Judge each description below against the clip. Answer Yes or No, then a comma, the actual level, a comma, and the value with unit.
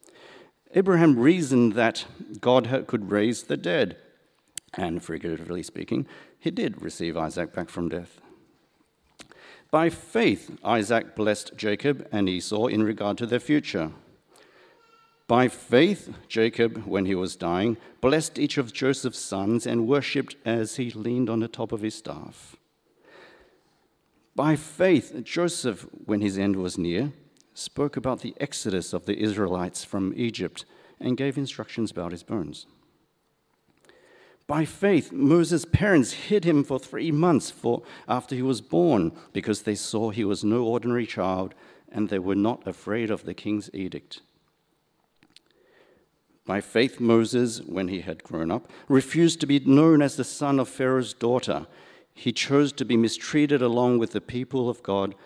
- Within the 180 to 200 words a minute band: No, average, 150 wpm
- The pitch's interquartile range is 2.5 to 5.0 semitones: No, wide, 5.6 semitones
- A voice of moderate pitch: No, low, 120 Hz